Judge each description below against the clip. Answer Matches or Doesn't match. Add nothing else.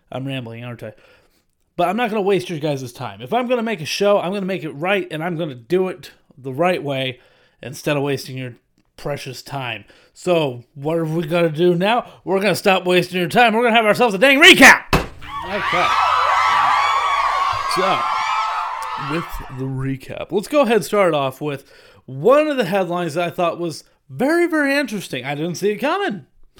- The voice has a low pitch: Doesn't match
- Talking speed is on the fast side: Matches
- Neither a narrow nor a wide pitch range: Doesn't match